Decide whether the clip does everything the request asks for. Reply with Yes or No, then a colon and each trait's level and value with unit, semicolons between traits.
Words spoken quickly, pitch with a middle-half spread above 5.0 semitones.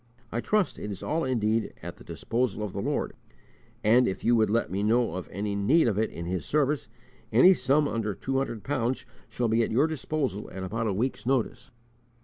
No: fast, 210 wpm; average, 4.2 semitones